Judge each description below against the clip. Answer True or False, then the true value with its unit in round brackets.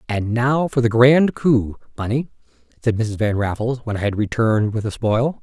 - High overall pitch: False (115 Hz)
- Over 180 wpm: True (200 wpm)